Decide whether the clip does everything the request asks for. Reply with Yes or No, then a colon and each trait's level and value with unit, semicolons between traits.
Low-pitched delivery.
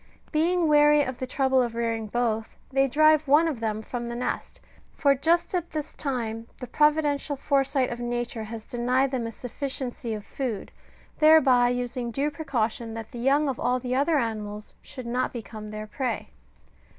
No: very high, 250 Hz